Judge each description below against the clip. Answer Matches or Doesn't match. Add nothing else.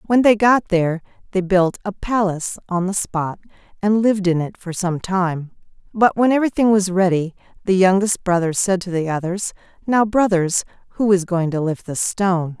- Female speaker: Matches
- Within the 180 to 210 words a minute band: Matches